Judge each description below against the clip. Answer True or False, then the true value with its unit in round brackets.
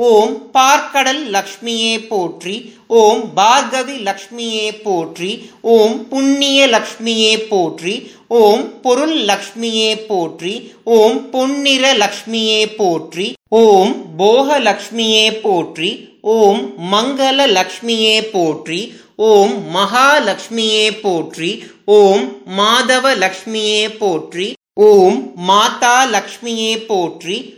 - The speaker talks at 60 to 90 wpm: True (85 wpm)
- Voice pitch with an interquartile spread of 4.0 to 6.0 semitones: False (3.0 semitones)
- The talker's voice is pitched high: True (220 Hz)